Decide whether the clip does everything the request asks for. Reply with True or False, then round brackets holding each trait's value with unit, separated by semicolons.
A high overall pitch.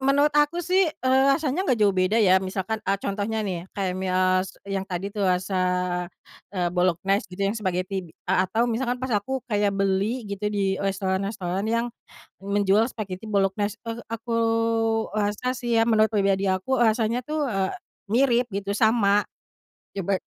True (205 Hz)